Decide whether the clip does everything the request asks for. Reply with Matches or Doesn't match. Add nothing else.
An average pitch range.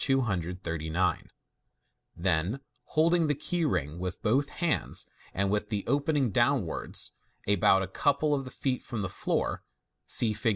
Doesn't match